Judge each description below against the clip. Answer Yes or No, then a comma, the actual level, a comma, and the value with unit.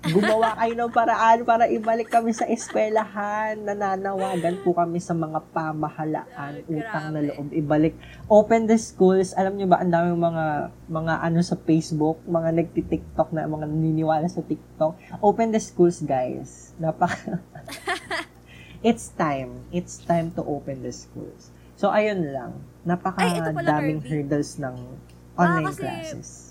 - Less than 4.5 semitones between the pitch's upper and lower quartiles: Yes, average, 4.0 semitones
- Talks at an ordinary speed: Yes, average, 140 wpm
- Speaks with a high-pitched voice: No, medium, 165 Hz